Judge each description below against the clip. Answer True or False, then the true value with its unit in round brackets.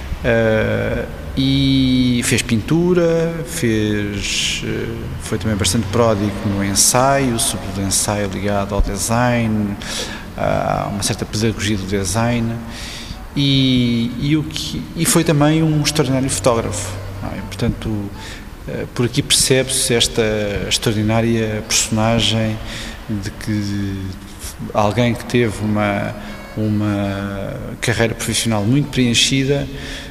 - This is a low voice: True (110 Hz)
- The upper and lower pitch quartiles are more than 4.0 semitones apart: False (3.2 semitones)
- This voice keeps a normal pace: False (110 wpm)